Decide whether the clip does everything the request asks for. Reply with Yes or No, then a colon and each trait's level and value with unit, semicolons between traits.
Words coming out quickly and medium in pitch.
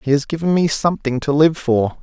Yes: fast, 235 wpm; medium, 145 Hz